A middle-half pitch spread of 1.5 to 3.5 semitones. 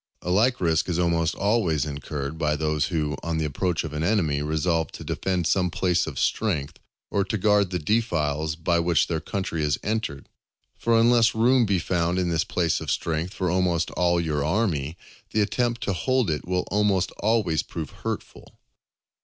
No: average, 4.3 semitones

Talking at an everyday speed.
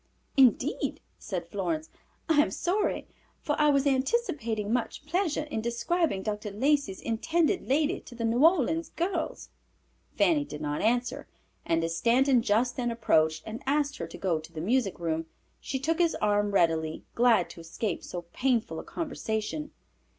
Yes: average, 160 wpm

